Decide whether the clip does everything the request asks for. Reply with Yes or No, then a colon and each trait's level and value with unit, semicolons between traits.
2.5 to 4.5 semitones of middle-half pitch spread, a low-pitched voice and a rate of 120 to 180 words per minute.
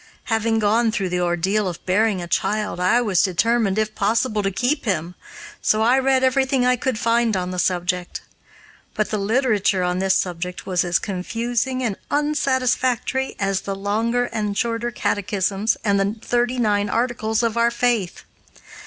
No: average, 3.8 semitones; high, 215 Hz; average, 165 wpm